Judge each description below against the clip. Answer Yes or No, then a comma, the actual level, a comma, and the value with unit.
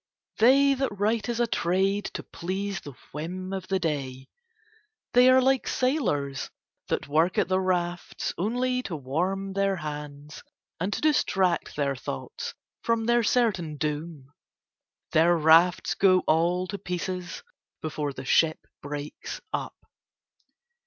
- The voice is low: No, medium, 180 Hz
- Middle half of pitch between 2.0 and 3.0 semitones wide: No, average, 5.1 semitones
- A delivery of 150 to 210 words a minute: No, slow, 135 wpm